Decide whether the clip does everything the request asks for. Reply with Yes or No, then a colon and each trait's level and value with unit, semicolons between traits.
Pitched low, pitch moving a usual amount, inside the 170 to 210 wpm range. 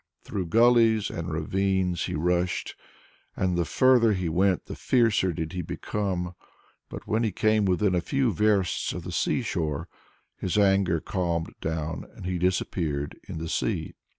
No: very low, 90 Hz; average, 3.8 semitones; average, 160 wpm